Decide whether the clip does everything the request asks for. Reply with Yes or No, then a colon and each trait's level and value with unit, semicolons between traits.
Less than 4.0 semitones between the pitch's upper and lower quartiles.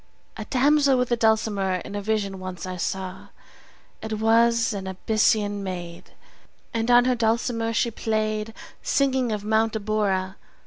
Yes: average, 2.7 semitones